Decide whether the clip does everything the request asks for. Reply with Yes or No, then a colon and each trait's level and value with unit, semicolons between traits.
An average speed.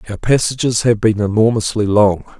Yes: average, 150 wpm